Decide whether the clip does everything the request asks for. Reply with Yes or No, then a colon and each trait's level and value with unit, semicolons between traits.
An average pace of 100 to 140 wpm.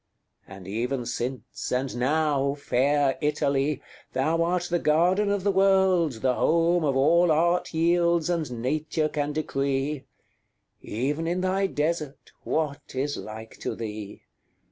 Yes: slow, 135 wpm